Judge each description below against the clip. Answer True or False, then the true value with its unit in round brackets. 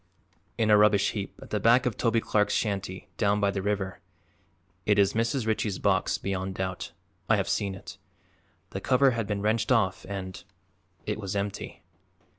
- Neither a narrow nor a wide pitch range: False (2.3 semitones)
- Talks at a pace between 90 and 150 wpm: False (175 wpm)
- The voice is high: False (105 Hz)